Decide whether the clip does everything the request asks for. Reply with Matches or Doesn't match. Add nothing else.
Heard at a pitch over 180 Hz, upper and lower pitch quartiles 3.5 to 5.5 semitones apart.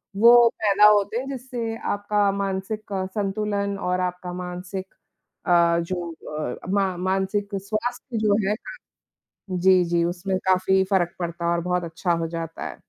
Doesn't match